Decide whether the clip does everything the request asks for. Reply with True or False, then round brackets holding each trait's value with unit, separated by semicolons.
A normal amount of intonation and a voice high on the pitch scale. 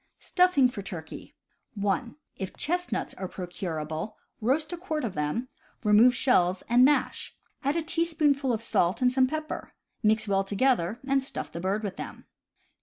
False (6.5 semitones; 235 Hz)